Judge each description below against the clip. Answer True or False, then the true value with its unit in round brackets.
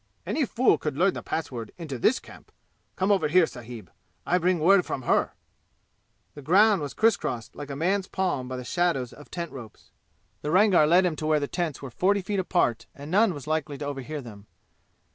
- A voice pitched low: False (155 Hz)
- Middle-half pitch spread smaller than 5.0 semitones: False (5.3 semitones)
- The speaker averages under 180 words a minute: False (205 wpm)